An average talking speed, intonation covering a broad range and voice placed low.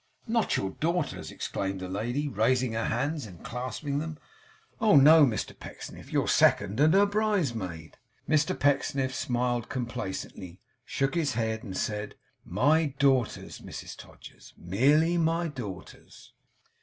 No: slow, 130 wpm; wide, 6.3 semitones; low, 130 Hz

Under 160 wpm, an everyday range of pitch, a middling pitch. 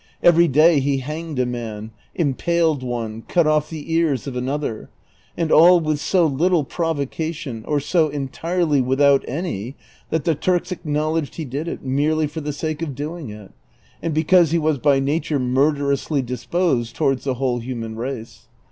No: average, 165 wpm; average, 3.7 semitones; medium, 145 Hz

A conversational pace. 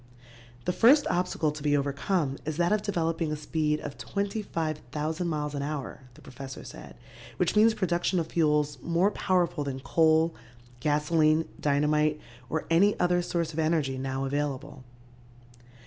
Yes: average, 150 wpm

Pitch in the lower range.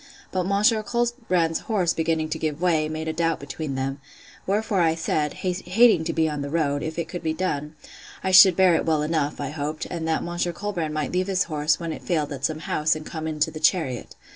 No: medium, 160 Hz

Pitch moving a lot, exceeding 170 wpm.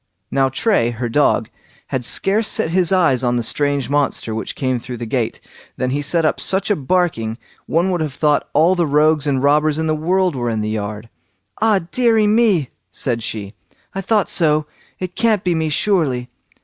Yes: wide, 6.4 semitones; average, 195 wpm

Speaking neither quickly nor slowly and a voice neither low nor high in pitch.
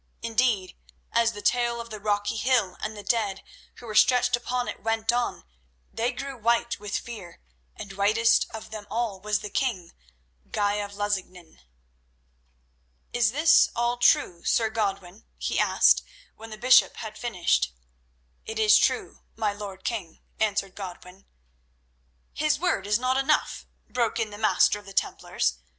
No: average, 155 wpm; high, 215 Hz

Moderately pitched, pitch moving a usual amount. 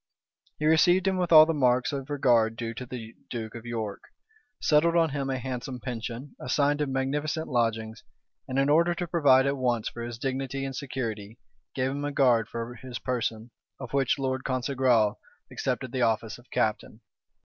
No: low, 130 Hz; average, 3.3 semitones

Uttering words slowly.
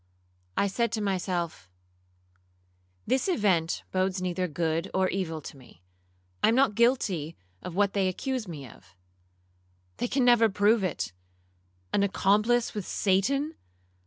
Yes: slow, 130 wpm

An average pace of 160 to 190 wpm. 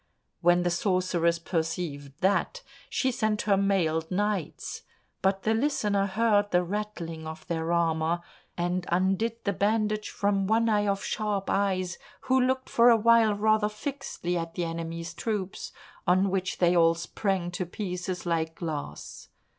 No: average, 150 wpm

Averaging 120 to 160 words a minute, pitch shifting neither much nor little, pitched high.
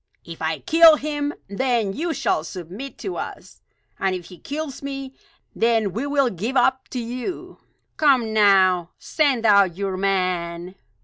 No: average, 150 wpm; wide, 6.7 semitones; high, 225 Hz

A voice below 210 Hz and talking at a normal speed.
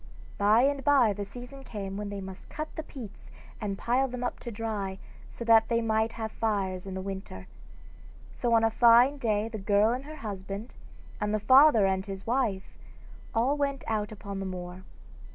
No: high, 220 Hz; average, 190 wpm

